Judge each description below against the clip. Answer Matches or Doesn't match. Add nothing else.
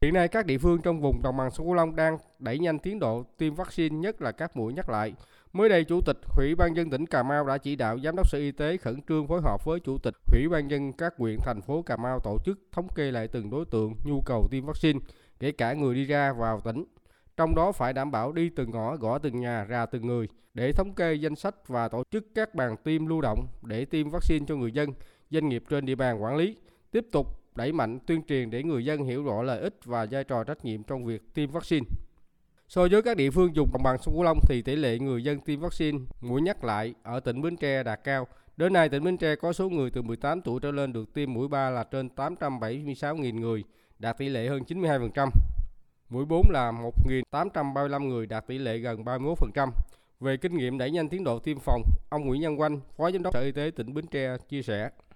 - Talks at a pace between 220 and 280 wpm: Matches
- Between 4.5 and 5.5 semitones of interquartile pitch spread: Matches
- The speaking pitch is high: Doesn't match